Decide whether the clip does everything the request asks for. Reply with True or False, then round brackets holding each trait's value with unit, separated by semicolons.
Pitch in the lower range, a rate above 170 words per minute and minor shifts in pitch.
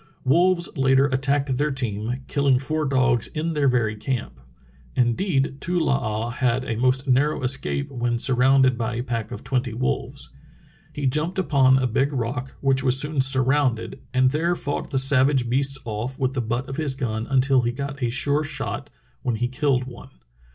True (130 Hz; 185 wpm; 2.2 semitones)